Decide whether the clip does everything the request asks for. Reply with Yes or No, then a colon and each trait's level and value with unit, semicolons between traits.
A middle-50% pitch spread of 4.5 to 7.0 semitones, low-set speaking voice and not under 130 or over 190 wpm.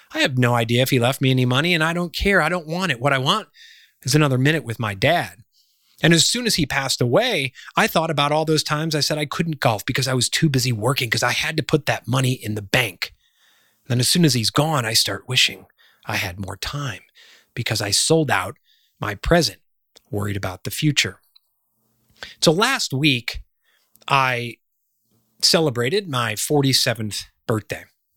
No: average, 5.2 semitones; low, 130 Hz; average, 200 wpm